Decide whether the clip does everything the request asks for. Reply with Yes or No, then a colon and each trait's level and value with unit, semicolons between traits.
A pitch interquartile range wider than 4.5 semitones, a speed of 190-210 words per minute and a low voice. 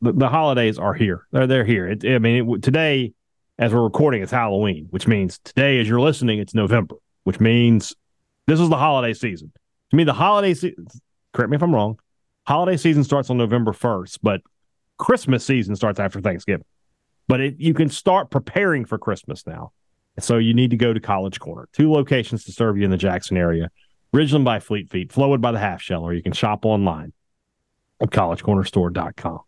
Yes: average, 5.3 semitones; average, 200 wpm; low, 120 Hz